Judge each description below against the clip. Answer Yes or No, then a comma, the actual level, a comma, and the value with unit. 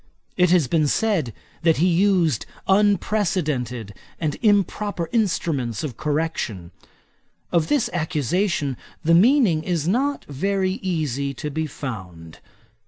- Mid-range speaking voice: Yes, medium, 165 Hz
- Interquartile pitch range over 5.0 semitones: Yes, wide, 5.6 semitones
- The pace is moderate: No, slow, 115 wpm